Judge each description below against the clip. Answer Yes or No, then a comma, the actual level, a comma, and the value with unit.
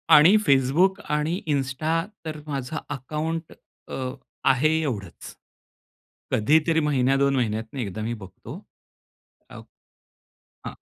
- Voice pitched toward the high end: No, medium, 140 Hz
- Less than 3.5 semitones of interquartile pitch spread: No, average, 3.9 semitones